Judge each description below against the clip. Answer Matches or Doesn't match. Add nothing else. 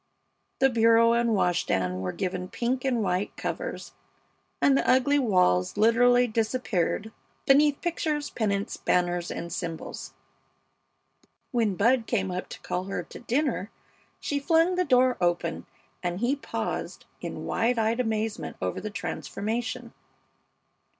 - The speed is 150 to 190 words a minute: Doesn't match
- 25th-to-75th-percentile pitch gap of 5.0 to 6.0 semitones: Matches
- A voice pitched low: Doesn't match